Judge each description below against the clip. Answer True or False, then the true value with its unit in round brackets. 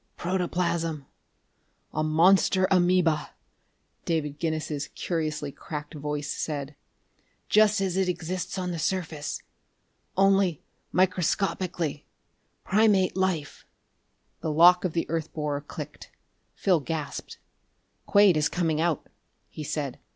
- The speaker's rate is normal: False (105 wpm)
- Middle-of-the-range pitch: True (165 Hz)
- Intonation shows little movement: False (3.4 semitones)